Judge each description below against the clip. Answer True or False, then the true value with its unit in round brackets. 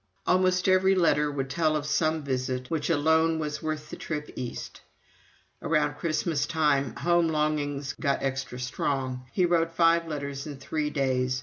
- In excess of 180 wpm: False (160 wpm)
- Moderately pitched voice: True (150 Hz)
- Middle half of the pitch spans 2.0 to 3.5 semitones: True (3.0 semitones)